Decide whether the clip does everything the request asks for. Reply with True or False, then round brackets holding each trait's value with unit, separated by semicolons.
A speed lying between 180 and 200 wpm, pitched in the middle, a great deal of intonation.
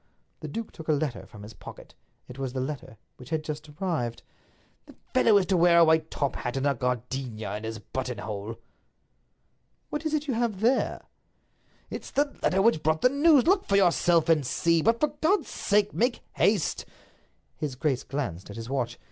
True (185 wpm; 155 Hz; 8.5 semitones)